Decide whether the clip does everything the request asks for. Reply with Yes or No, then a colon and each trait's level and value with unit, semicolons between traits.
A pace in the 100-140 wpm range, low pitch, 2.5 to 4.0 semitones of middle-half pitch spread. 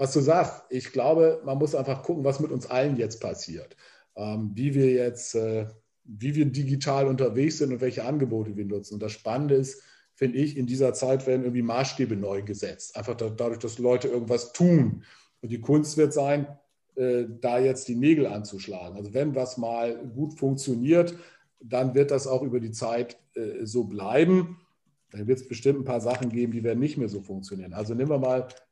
No: fast, 190 wpm; low, 130 Hz; average, 3.1 semitones